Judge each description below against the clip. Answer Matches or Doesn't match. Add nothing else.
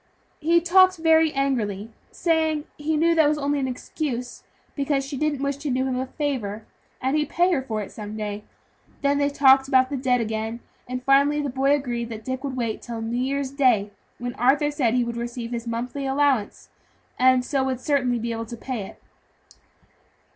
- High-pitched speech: Matches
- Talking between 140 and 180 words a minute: Doesn't match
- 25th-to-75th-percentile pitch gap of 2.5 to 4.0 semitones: Matches